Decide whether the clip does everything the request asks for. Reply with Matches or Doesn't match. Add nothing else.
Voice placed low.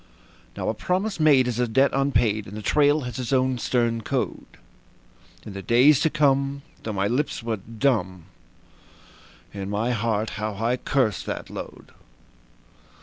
Matches